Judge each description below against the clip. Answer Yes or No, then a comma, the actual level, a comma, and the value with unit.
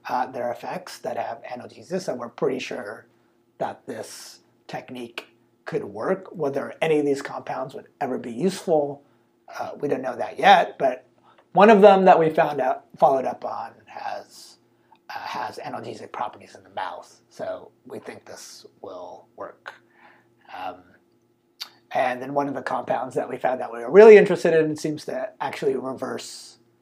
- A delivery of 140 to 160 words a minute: No, average, 170 wpm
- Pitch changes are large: Yes, wide, 7.2 semitones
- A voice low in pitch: No, medium, 155 Hz